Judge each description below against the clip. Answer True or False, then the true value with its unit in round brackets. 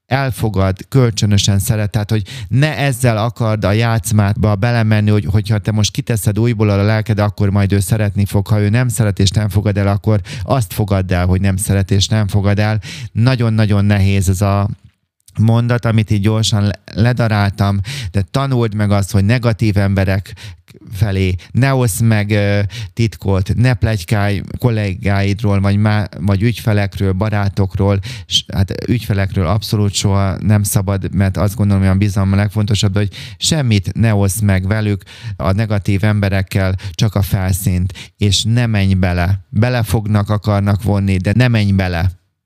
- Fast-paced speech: True (160 wpm)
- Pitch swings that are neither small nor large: False (1.9 semitones)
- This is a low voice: True (105 Hz)